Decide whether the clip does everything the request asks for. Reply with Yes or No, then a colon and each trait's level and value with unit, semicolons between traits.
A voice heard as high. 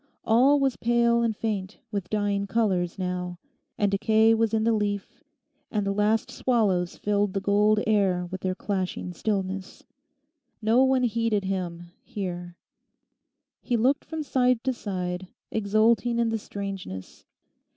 Yes: high, 205 Hz